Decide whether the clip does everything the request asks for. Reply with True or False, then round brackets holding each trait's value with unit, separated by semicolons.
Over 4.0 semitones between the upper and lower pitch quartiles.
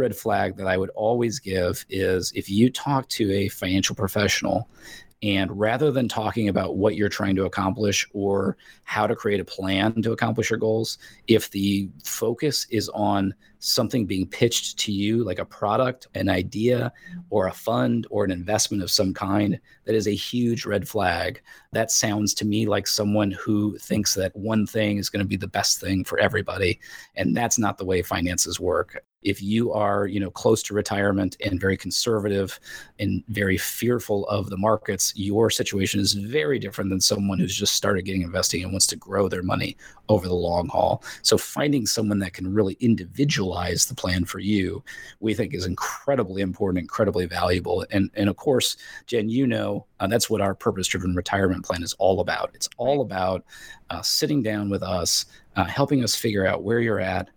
False (2.7 semitones)